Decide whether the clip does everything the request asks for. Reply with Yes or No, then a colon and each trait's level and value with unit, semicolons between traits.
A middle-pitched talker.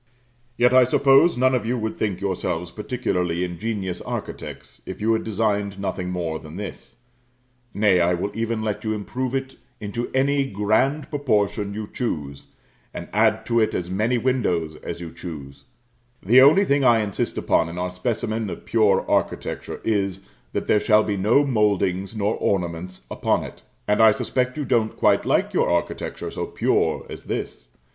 No: low, 105 Hz